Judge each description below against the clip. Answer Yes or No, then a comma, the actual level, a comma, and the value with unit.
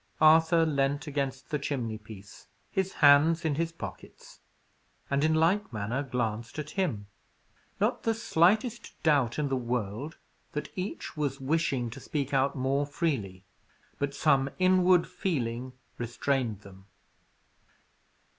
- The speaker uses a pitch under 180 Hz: Yes, medium, 140 Hz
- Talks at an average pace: No, slow, 125 wpm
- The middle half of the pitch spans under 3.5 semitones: No, average, 4.8 semitones